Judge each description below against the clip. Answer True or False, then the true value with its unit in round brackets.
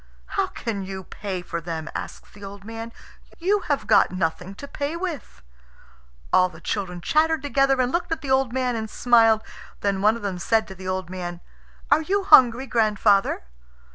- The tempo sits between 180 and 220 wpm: True (185 wpm)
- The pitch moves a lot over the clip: True (6.1 semitones)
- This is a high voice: True (220 Hz)